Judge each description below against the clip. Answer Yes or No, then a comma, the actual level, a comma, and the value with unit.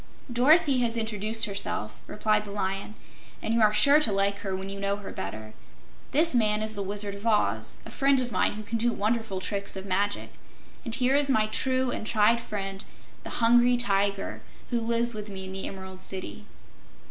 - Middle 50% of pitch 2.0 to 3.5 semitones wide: Yes, average, 3.1 semitones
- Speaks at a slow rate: No, average, 195 wpm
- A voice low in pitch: No, high, 210 Hz